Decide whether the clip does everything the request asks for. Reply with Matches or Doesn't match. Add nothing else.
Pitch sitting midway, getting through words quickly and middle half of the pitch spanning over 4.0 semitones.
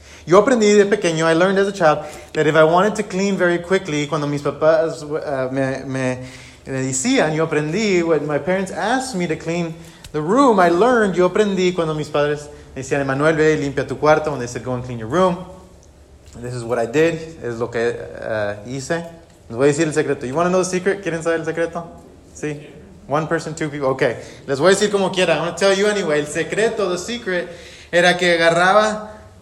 Matches